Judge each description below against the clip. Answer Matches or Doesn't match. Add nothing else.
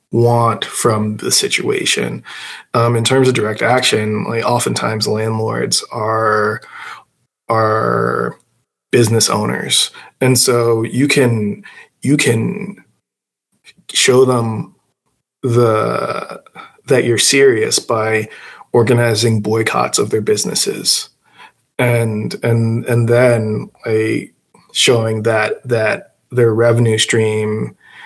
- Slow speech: Matches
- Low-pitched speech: Matches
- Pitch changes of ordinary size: Doesn't match